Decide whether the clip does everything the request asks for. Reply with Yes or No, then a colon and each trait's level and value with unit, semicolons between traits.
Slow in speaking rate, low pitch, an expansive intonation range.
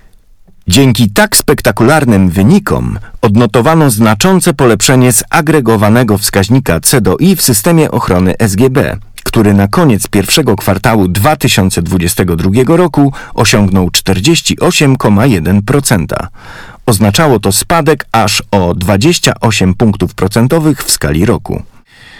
Yes: slow, 95 wpm; low, 115 Hz; wide, 6.2 semitones